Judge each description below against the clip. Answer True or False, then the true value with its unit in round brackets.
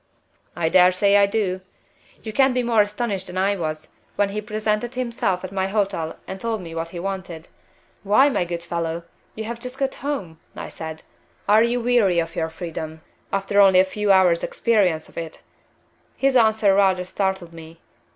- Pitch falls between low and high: False (195 Hz)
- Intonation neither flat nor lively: True (4.1 semitones)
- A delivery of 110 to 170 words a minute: False (185 wpm)